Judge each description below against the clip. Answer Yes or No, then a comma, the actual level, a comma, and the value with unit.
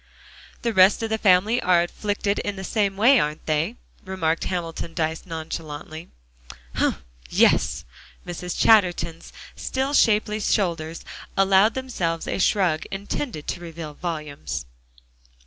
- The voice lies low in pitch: No, medium, 180 Hz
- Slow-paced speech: Yes, slow, 125 wpm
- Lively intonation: No, average, 4.2 semitones